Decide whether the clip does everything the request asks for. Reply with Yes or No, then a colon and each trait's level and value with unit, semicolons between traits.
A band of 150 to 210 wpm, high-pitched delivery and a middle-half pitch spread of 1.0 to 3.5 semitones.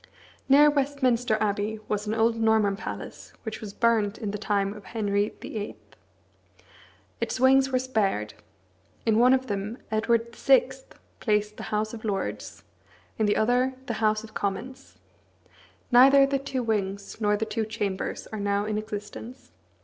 Yes: average, 155 wpm; high, 220 Hz; average, 3.1 semitones